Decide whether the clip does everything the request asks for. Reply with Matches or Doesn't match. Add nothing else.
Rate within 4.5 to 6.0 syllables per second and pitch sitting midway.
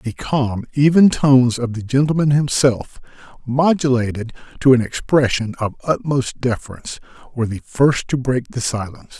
Doesn't match